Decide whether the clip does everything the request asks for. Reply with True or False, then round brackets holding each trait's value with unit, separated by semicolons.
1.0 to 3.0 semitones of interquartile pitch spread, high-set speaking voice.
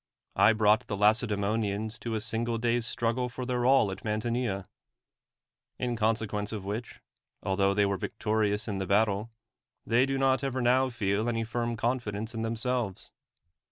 False (2.5 semitones; 110 Hz)